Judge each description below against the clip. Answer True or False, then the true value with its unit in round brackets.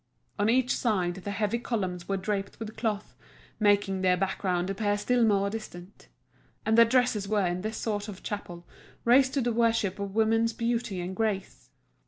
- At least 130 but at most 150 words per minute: False (175 wpm)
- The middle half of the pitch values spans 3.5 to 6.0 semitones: False (2.9 semitones)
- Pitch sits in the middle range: False (205 Hz)